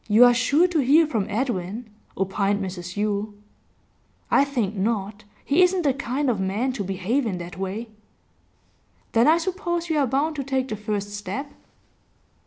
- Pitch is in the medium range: No, high, 230 Hz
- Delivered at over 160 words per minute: Yes, average, 170 wpm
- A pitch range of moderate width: No, wide, 5.8 semitones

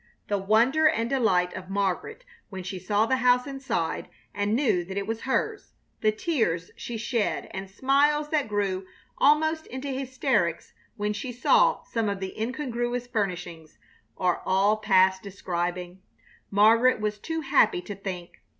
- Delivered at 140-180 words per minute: Yes, average, 150 wpm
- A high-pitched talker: Yes, high, 215 Hz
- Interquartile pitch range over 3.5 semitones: Yes, wide, 5.6 semitones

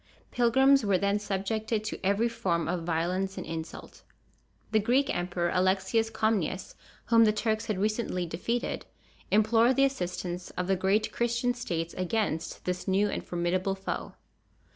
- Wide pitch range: No, average, 3.8 semitones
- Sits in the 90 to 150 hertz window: No, high, 200 Hz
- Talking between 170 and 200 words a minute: No, average, 145 wpm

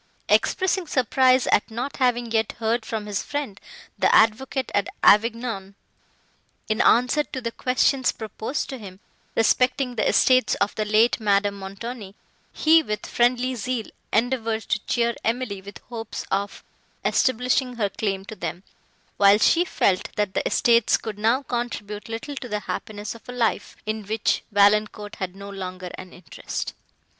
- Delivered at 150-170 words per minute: Yes, average, 155 wpm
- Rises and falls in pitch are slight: No, average, 3.5 semitones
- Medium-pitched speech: No, high, 225 Hz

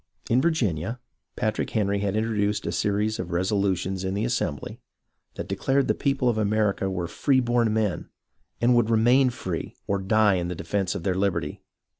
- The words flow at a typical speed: Yes, average, 175 wpm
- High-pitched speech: No, low, 105 Hz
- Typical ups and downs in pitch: Yes, average, 3.5 semitones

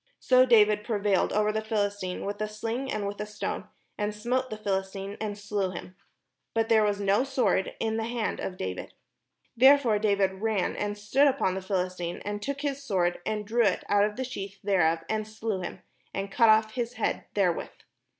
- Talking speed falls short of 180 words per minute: No, average, 200 wpm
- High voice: Yes, high, 210 Hz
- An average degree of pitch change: No, narrow, 2.3 semitones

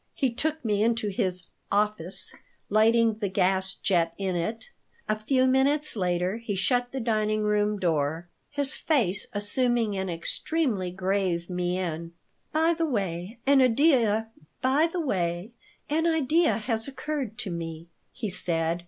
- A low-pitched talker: No, high, 215 Hz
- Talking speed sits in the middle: No, slow, 125 wpm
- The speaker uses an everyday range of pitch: No, wide, 6.0 semitones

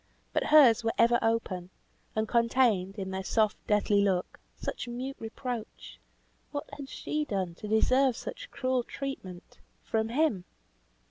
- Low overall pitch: No, high, 225 Hz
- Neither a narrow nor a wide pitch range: Yes, average, 4.3 semitones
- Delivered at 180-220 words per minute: No, average, 140 wpm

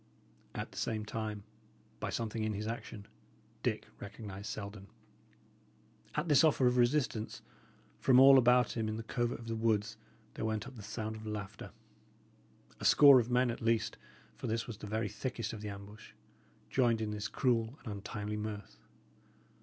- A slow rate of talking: No, average, 170 wpm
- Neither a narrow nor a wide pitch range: No, narrow, 2.2 semitones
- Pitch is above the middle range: No, low, 110 Hz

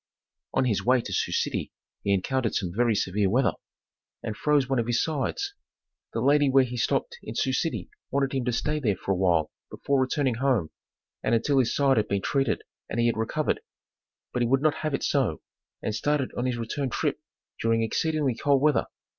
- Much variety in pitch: No, average, 3.8 semitones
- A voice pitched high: No, low, 125 Hz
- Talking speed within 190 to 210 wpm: Yes, fast, 205 wpm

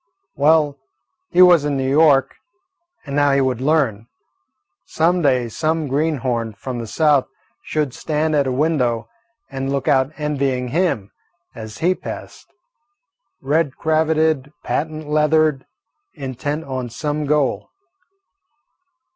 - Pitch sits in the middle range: Yes, medium, 145 Hz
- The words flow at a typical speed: No, slow, 120 wpm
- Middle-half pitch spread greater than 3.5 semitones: No, average, 3.1 semitones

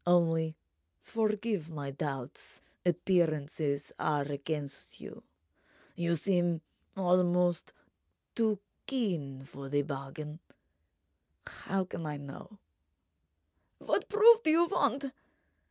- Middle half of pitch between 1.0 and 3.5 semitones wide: No, average, 5.1 semitones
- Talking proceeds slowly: Yes, slow, 85 wpm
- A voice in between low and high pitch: Yes, medium, 165 Hz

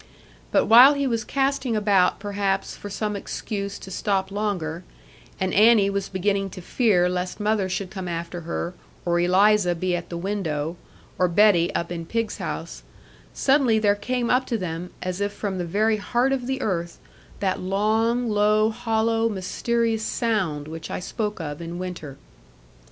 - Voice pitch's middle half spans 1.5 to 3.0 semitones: No, average, 3.7 semitones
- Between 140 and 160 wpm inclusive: No, average, 170 wpm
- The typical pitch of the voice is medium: No, high, 200 Hz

